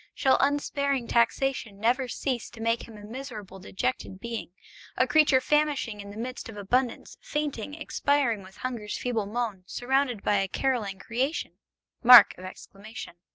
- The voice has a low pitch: No, high, 240 Hz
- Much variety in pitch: No, average, 4.4 semitones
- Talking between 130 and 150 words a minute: Yes, average, 140 wpm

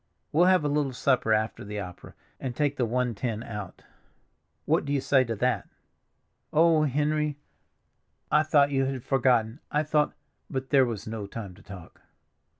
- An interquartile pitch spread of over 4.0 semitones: Yes, average, 4.7 semitones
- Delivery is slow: No, average, 170 wpm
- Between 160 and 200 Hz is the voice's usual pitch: No, low, 130 Hz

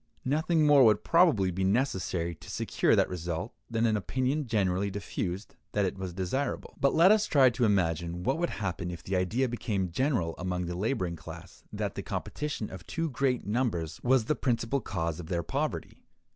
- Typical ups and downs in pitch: No, wide, 6.7 semitones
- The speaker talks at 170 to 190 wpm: Yes, average, 185 wpm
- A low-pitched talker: Yes, low, 105 Hz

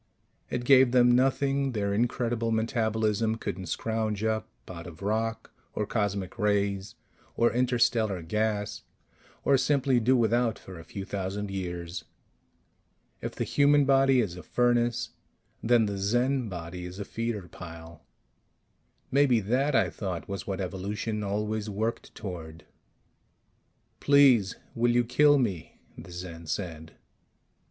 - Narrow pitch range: No, average, 4.1 semitones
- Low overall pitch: Yes, low, 110 Hz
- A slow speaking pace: Yes, slow, 130 wpm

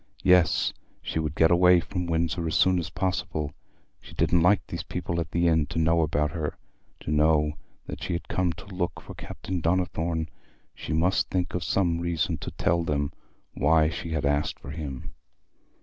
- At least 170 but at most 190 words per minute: Yes, average, 185 wpm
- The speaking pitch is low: Yes, very low, 85 Hz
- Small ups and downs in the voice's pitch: Yes, narrow, 2.2 semitones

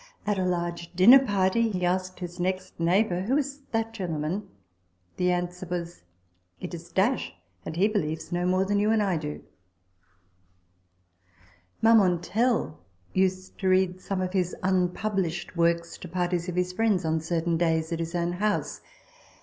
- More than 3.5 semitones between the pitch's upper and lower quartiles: No, narrow, 2.4 semitones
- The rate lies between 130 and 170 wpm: Yes, average, 165 wpm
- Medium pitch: Yes, medium, 180 Hz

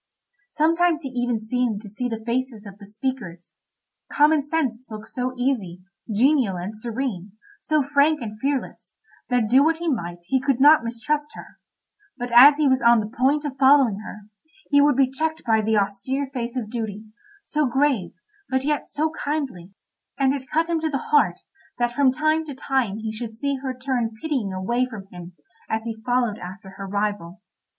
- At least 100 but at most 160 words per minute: No, average, 185 wpm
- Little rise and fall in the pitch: No, average, 4.8 semitones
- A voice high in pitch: Yes, very high, 250 Hz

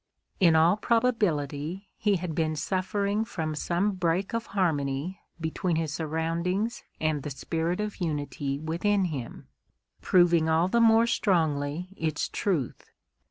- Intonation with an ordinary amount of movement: Yes, average, 4.0 semitones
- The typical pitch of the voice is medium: Yes, medium, 170 Hz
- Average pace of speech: No, slow, 130 wpm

